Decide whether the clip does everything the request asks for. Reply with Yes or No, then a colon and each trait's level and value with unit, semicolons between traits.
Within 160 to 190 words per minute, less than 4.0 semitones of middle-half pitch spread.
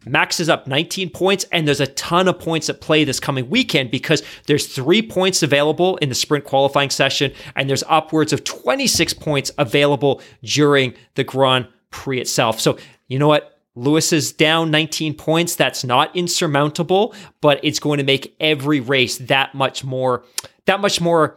Yes: average, 175 wpm; average, 3.1 semitones